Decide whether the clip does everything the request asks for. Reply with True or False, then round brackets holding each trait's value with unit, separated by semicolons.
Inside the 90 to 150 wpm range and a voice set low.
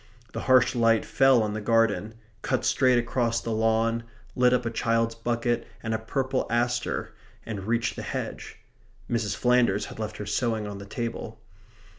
False (170 wpm; 115 Hz)